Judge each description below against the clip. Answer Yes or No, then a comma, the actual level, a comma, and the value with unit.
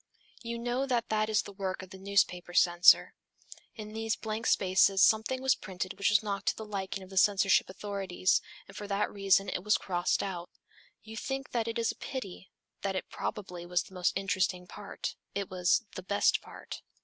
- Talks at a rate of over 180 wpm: Yes, average, 195 wpm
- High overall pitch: Yes, high, 200 Hz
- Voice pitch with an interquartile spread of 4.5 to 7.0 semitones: No, narrow, 2.6 semitones